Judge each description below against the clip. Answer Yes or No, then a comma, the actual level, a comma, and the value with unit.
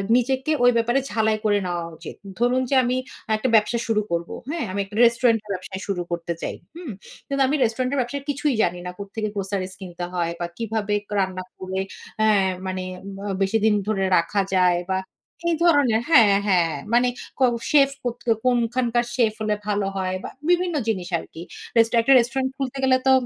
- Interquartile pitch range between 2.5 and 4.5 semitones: No, average, 5.0 semitones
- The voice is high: Yes, high, 220 Hz